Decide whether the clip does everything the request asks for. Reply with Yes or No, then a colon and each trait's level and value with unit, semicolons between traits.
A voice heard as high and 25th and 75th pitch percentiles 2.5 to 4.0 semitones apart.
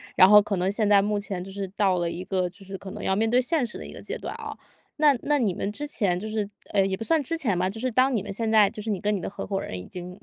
Yes: high, 205 Hz; average, 2.8 semitones